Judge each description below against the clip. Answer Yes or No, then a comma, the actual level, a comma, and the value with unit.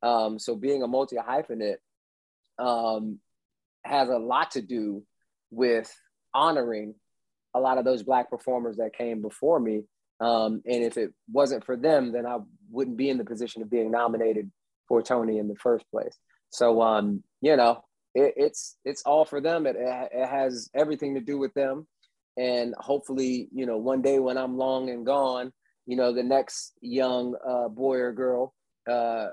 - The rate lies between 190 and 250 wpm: No, average, 175 wpm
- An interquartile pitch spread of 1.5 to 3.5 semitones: Yes, narrow, 2.4 semitones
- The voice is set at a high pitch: No, low, 125 Hz